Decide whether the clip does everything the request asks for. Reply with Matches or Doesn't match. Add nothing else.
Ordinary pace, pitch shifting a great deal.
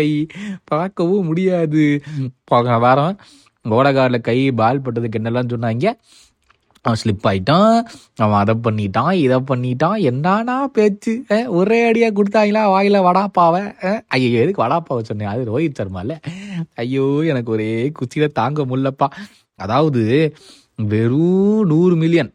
Matches